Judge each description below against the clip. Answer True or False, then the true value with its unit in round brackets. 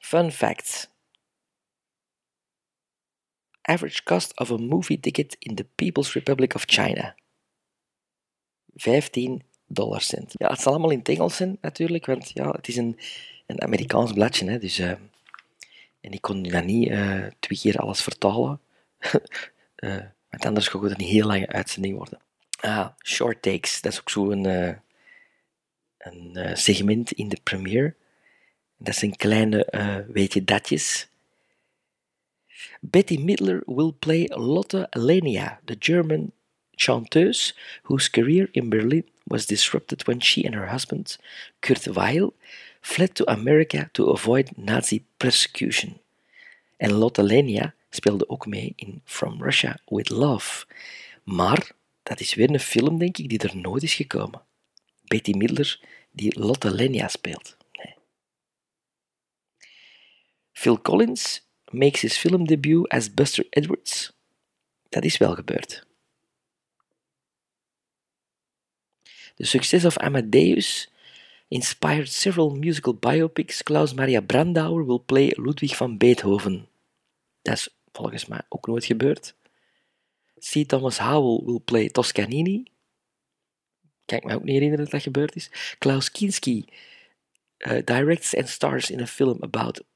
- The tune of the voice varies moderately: False (7.1 semitones)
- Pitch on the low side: True (125 Hz)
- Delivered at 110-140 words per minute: True (135 wpm)